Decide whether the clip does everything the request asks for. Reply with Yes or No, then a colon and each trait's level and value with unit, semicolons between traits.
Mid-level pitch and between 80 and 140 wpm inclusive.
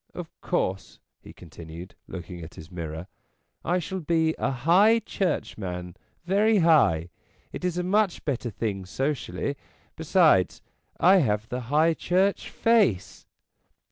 Yes: medium, 145 Hz; slow, 135 wpm